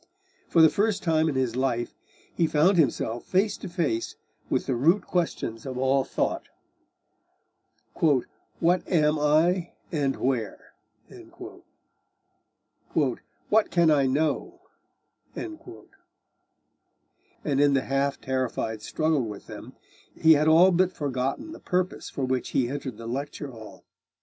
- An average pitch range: Yes, average, 4.6 semitones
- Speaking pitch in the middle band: Yes, medium, 145 Hz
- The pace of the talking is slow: Yes, slow, 125 wpm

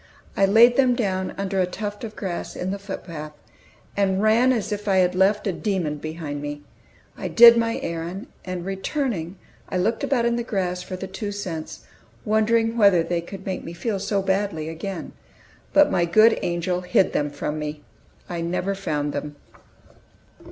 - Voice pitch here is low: No, high, 190 Hz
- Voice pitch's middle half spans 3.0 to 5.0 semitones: Yes, average, 3.7 semitones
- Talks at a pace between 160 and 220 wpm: Yes, average, 180 wpm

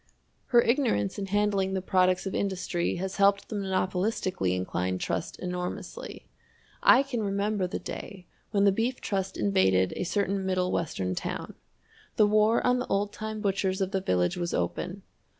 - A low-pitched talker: No, high, 190 Hz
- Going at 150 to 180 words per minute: Yes, average, 165 wpm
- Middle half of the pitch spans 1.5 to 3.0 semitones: Yes, narrow, 2.5 semitones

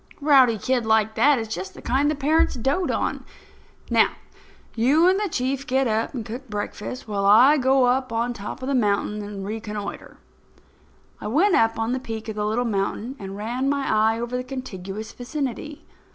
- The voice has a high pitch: Yes, high, 240 Hz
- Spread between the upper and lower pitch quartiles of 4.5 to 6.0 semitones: No, average, 3.8 semitones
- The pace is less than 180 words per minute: No, average, 195 wpm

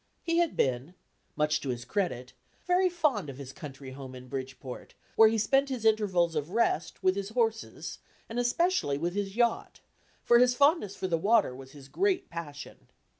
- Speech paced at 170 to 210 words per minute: Yes, average, 180 wpm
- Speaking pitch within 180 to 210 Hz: Yes, high, 190 Hz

